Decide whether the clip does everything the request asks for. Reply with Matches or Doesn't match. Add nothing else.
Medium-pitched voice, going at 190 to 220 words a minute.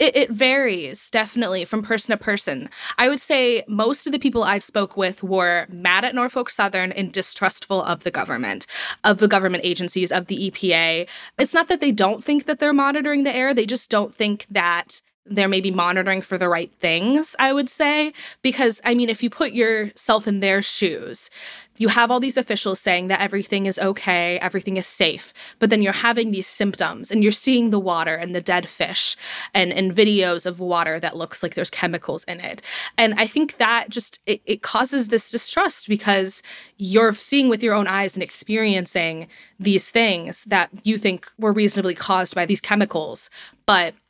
Doesn't match